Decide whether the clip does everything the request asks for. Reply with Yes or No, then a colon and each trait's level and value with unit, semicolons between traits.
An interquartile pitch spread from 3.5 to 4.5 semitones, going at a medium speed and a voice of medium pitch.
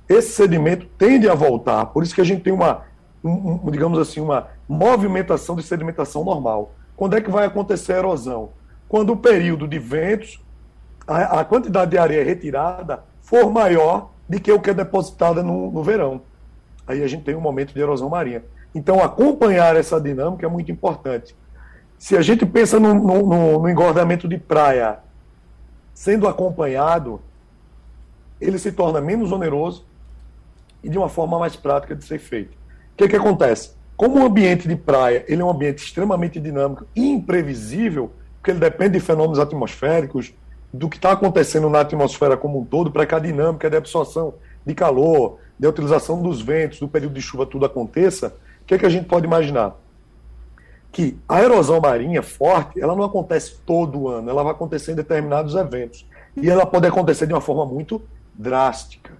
No: average, 5.0 semitones; average, 175 wpm; medium, 160 Hz